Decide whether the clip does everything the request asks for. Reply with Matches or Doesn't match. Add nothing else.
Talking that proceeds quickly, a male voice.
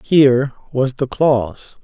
Doesn't match